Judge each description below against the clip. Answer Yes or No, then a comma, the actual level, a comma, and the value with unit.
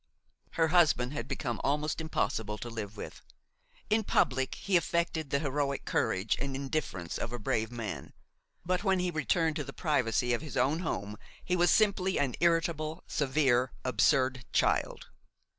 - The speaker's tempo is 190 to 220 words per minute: No, average, 160 wpm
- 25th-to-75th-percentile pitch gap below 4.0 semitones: No, average, 5.2 semitones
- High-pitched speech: No, medium, 140 Hz